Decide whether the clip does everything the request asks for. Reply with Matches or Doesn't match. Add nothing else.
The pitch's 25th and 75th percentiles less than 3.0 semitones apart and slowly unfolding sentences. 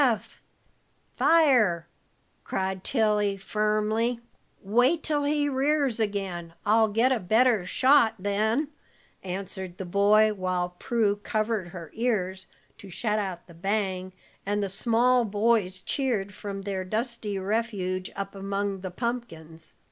Doesn't match